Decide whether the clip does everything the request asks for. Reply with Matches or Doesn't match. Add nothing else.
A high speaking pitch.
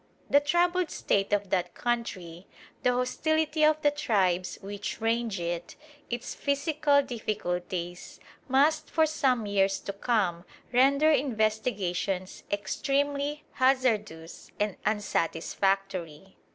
Matches